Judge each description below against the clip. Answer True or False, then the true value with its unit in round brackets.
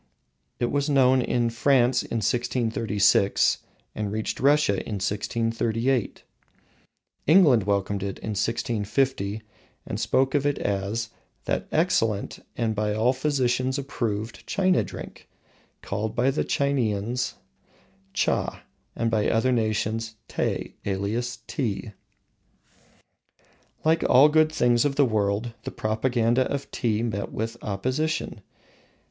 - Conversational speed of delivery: False (120 wpm)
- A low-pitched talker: True (115 Hz)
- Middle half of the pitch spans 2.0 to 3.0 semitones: False (3.6 semitones)